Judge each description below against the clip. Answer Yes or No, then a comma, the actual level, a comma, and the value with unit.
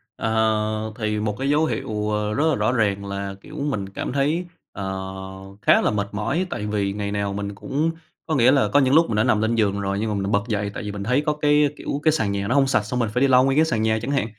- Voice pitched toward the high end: No, low, 110 Hz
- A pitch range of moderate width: Yes, average, 5.0 semitones